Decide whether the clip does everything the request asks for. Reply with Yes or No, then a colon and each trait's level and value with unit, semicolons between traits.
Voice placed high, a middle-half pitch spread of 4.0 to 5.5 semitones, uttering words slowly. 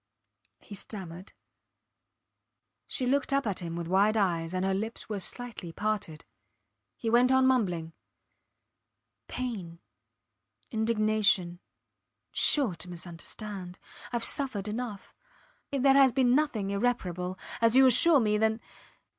Yes: high, 215 Hz; average, 5.1 semitones; slow, 125 wpm